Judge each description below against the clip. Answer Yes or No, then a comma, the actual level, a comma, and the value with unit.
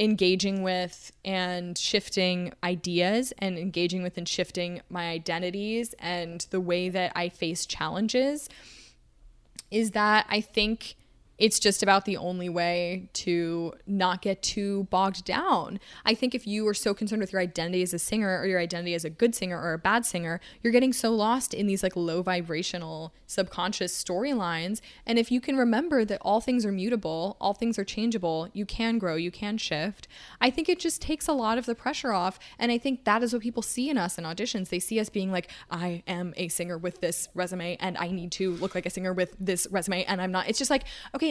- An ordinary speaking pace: No, fast, 210 wpm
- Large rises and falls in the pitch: No, average, 3.9 semitones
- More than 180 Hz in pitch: Yes, high, 190 Hz